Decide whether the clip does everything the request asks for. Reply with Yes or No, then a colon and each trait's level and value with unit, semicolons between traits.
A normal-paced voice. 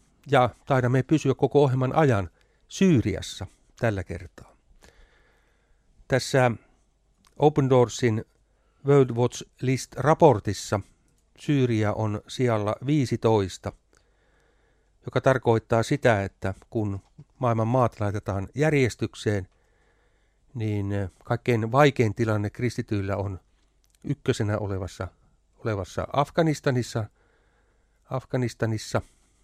No: slow, 80 wpm